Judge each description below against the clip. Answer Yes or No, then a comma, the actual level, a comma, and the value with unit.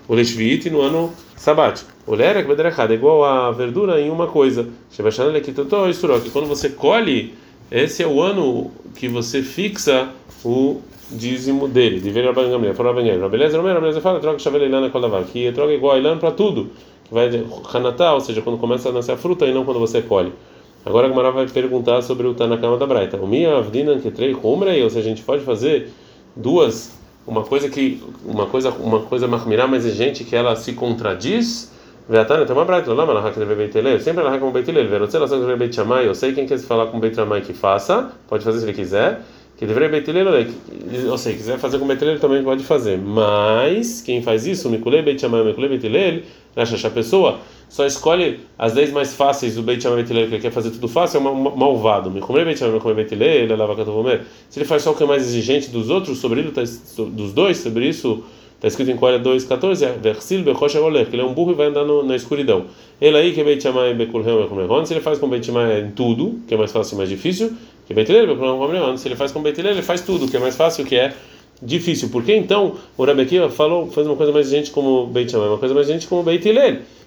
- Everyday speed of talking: No, fast, 245 wpm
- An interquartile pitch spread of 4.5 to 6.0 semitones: Yes, average, 4.8 semitones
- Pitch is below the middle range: Yes, low, 130 Hz